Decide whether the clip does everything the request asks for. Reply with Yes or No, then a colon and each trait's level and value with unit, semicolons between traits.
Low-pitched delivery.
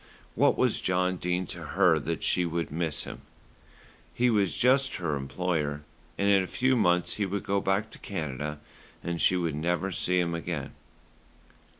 Yes: very low, 90 Hz